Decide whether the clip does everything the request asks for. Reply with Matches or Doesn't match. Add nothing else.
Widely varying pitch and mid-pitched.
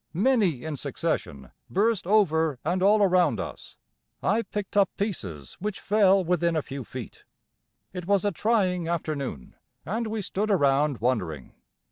Matches